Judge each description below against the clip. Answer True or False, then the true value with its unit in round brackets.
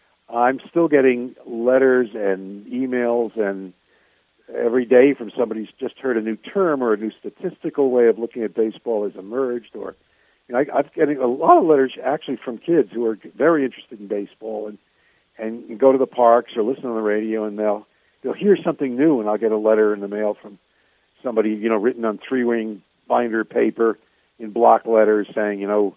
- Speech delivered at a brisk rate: True (210 wpm)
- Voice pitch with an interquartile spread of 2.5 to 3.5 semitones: True (3.0 semitones)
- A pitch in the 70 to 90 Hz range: False (115 Hz)